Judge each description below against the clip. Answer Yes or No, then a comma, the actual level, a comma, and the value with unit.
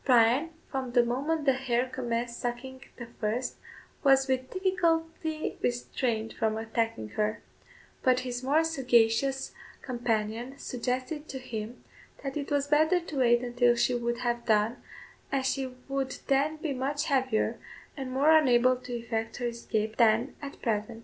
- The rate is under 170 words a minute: Yes, average, 150 wpm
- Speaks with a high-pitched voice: Yes, very high, 255 Hz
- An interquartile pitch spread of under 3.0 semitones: Yes, narrow, 2.6 semitones